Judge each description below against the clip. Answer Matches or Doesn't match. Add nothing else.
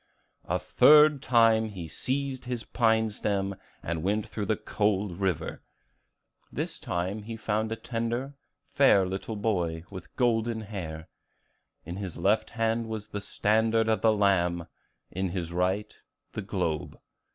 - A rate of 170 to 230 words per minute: Doesn't match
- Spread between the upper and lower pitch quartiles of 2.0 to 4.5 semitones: Matches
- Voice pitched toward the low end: Matches